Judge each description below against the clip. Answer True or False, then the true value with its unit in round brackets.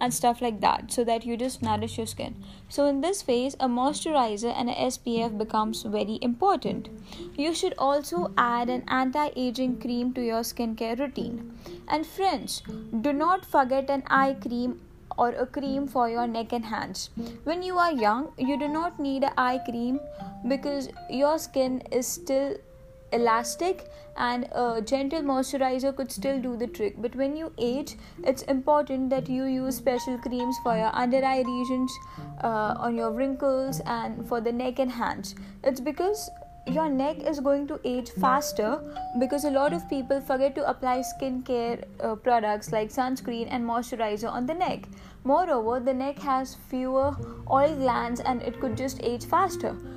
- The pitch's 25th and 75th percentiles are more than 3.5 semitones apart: False (2.9 semitones)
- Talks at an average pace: True (170 wpm)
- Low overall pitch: False (255 Hz)